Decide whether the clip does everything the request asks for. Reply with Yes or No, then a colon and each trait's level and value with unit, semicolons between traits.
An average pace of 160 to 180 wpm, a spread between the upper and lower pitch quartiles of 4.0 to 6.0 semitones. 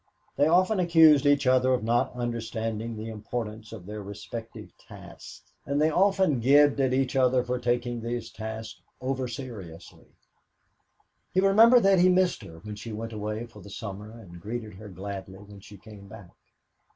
Yes: average, 175 wpm; average, 4.4 semitones